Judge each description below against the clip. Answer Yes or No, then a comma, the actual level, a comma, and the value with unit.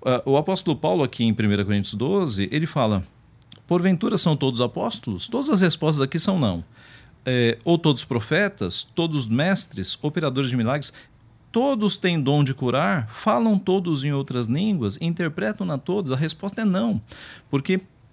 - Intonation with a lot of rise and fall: Yes, wide, 7.0 semitones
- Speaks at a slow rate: No, average, 150 wpm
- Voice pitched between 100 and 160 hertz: Yes, medium, 140 Hz